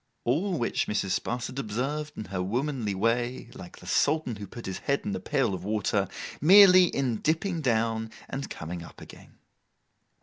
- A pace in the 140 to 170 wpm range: Yes, average, 160 wpm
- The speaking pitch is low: Yes, low, 120 Hz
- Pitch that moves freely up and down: Yes, wide, 6.0 semitones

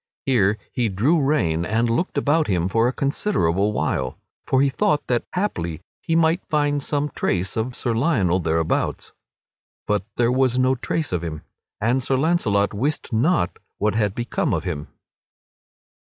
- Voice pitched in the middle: No, low, 120 Hz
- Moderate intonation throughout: No, wide, 6.8 semitones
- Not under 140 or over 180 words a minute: Yes, average, 160 wpm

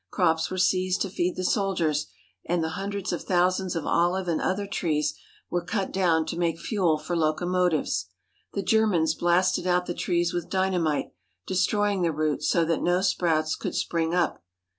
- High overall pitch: No, medium, 175 Hz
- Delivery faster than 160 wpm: Yes, average, 170 wpm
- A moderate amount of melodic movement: No, narrow, 2.3 semitones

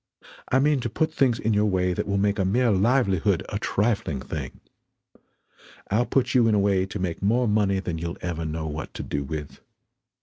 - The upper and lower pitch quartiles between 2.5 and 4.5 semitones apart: No, average, 4.9 semitones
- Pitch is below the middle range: Yes, low, 100 Hz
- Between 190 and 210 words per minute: Yes, fast, 205 wpm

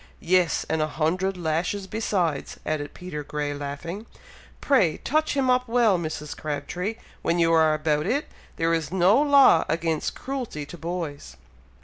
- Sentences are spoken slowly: No, average, 150 wpm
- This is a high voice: No, medium, 170 Hz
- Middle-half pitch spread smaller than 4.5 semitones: No, average, 4.8 semitones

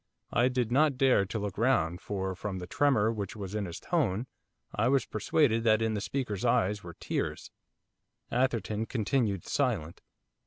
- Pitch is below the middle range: Yes, low, 110 Hz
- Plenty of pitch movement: No, average, 4.2 semitones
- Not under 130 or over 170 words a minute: Yes, average, 165 wpm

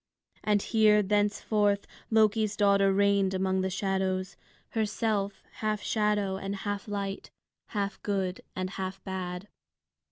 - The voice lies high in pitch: Yes, high, 200 Hz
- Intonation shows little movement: Yes, narrow, 1.6 semitones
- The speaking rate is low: Yes, slow, 120 wpm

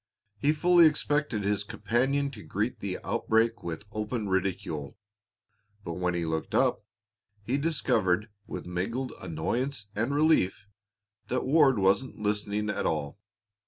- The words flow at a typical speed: No, slow, 130 wpm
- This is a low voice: Yes, low, 105 Hz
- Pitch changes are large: Yes, wide, 6.0 semitones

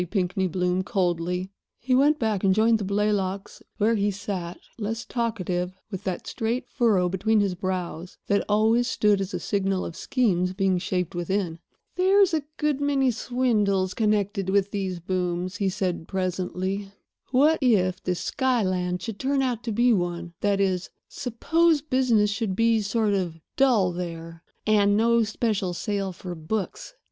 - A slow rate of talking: No, average, 155 wpm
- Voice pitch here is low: No, high, 200 Hz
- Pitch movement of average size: Yes, average, 3.8 semitones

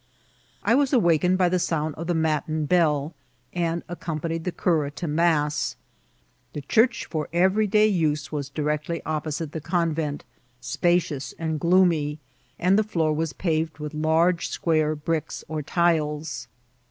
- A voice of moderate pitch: Yes, medium, 160 Hz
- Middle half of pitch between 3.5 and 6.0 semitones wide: No, narrow, 2.5 semitones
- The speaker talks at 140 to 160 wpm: Yes, average, 150 wpm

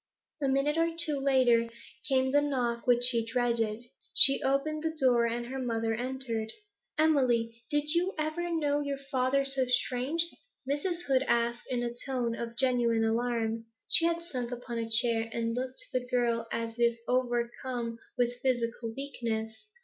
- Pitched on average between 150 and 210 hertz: No, very high, 250 Hz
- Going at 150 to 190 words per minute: Yes, average, 165 wpm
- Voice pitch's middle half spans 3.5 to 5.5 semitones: No, average, 2.9 semitones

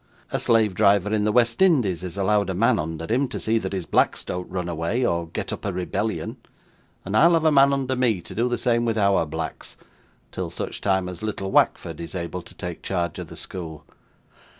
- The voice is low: Yes, low, 100 Hz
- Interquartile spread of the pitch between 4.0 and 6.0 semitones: Yes, average, 4.8 semitones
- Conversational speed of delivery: No, fast, 220 wpm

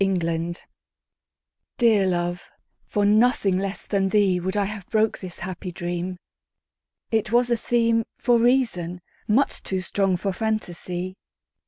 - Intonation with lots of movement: No, average, 3.6 semitones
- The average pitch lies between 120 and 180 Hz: No, high, 195 Hz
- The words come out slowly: Yes, slow, 125 wpm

